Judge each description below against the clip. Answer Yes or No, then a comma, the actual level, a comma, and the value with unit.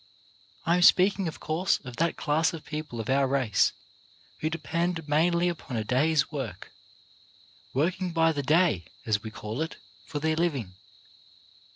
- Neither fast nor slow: Yes, average, 170 wpm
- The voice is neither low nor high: Yes, medium, 150 Hz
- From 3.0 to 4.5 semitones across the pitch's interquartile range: No, average, 5.3 semitones